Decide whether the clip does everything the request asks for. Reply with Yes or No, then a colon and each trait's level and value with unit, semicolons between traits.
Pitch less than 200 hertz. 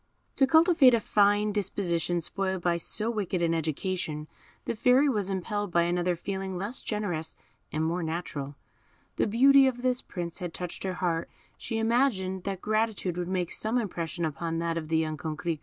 Yes: medium, 185 Hz